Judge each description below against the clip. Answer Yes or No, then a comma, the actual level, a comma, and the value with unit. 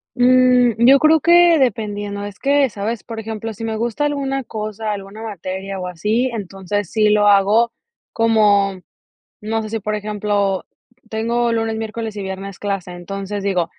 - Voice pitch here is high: Yes, high, 215 Hz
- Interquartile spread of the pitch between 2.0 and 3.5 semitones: Yes, narrow, 2.6 semitones